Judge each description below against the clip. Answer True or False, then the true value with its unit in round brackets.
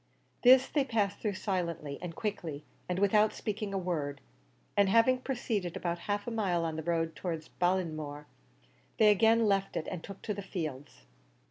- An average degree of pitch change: True (4.4 semitones)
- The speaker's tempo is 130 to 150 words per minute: False (170 wpm)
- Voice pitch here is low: False (190 Hz)